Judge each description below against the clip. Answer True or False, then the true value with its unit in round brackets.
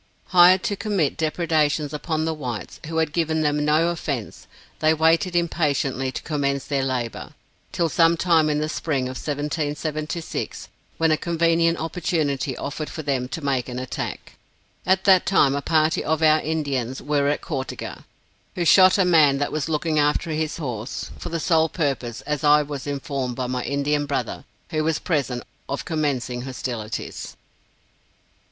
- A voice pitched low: False (150 Hz)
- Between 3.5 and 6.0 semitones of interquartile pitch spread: False (2.8 semitones)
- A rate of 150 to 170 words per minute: True (165 wpm)